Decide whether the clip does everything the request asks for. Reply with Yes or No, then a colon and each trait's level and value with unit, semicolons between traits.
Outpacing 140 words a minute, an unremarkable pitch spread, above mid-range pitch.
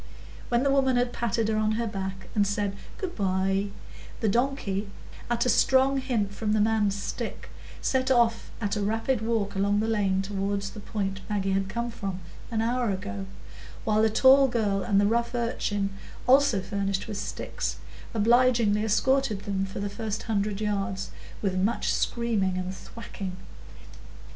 Yes: average, 165 wpm; average, 3.1 semitones; high, 210 Hz